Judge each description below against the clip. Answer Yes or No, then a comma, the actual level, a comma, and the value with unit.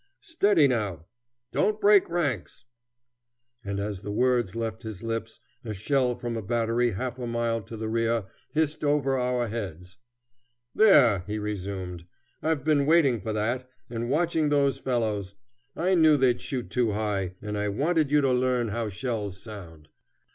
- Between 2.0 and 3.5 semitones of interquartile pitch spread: No, average, 4.8 semitones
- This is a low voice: Yes, low, 115 Hz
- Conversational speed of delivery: Yes, average, 160 wpm